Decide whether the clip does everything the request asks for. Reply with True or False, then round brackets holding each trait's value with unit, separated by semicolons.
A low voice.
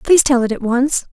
False (255 Hz)